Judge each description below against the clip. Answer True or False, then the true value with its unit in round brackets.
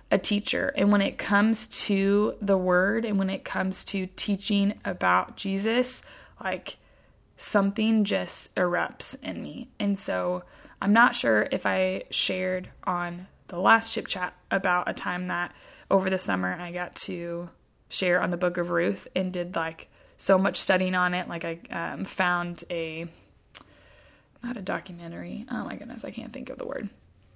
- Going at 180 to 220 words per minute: False (170 wpm)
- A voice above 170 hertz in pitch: True (185 Hz)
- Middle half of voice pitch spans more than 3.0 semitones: False (2.7 semitones)